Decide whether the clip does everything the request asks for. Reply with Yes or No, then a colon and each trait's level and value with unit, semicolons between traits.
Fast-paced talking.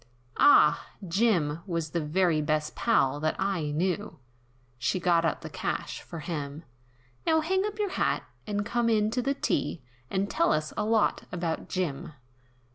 No: average, 165 wpm